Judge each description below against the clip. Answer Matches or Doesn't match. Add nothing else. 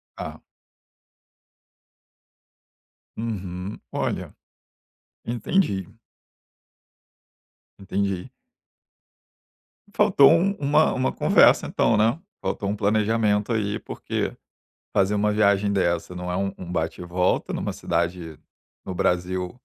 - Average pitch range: Matches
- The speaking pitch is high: Doesn't match